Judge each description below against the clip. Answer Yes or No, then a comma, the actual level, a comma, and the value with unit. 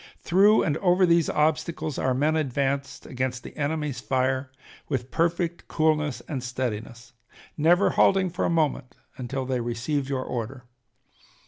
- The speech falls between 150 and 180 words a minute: No, average, 140 wpm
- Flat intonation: No, average, 3.9 semitones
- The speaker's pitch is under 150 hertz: Yes, medium, 140 Hz